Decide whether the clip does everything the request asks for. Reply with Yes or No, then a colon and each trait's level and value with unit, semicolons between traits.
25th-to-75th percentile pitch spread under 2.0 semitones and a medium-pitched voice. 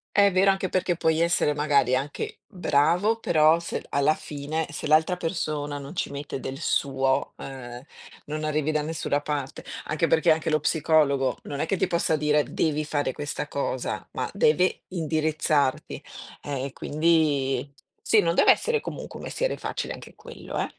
No: average, 2.8 semitones; medium, 155 Hz